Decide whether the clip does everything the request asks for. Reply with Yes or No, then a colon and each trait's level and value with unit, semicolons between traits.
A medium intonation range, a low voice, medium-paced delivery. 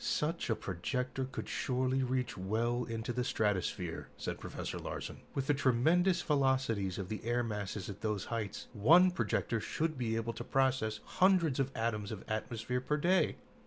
Yes: average, 3.7 semitones; low, 120 Hz; average, 165 wpm